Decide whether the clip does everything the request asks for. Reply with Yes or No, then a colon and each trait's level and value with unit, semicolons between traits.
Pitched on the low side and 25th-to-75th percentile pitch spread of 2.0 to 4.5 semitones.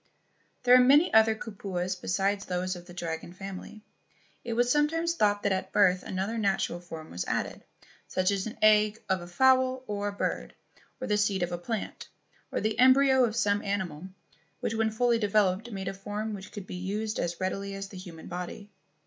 No: high, 205 Hz; average, 3.2 semitones